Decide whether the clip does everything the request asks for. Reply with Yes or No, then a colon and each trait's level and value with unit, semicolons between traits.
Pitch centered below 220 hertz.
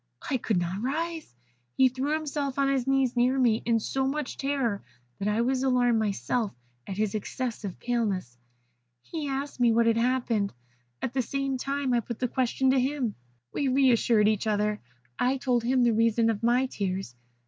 No: high, 245 Hz